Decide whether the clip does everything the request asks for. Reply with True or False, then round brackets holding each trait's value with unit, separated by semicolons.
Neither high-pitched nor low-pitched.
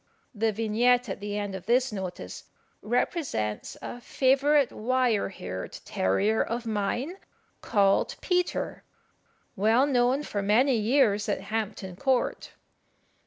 False (225 Hz)